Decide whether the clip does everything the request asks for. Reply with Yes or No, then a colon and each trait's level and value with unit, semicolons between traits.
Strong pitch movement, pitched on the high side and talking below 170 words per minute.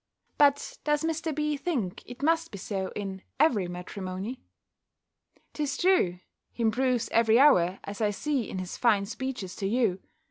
Yes: wide, 6.9 semitones; high, 230 Hz; average, 155 wpm